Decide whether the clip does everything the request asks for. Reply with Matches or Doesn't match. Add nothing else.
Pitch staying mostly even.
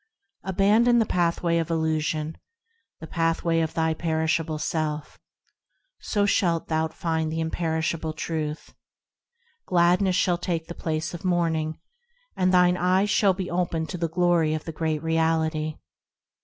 Matches